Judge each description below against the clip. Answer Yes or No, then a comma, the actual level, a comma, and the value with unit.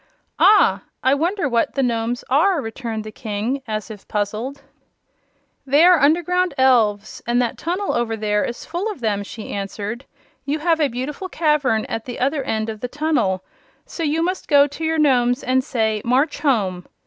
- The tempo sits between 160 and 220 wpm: Yes, average, 180 wpm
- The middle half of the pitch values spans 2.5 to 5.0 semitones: No, wide, 5.5 semitones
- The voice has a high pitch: Yes, very high, 255 Hz